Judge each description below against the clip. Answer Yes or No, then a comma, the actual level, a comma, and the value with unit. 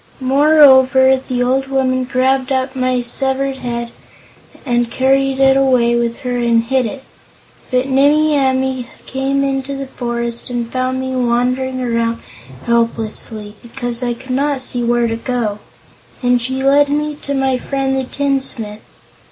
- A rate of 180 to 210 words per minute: No, average, 150 wpm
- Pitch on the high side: Yes, very high, 260 Hz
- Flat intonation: Yes, narrow, 2.0 semitones